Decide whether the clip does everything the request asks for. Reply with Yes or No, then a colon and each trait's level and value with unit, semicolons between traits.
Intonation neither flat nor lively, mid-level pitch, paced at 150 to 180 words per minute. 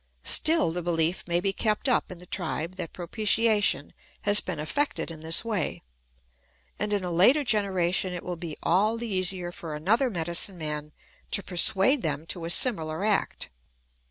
Yes: average, 4.0 semitones; medium, 180 Hz; average, 170 wpm